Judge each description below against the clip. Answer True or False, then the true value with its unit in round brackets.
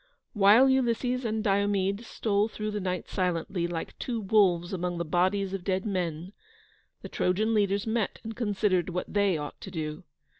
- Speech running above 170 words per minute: False (165 wpm)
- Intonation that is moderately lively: True (3.0 semitones)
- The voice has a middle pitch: False (195 Hz)